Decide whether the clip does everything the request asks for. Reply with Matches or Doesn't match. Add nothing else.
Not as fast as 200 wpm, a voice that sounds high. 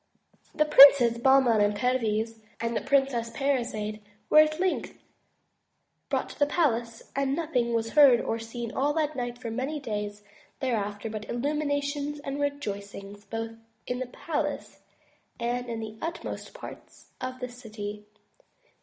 Matches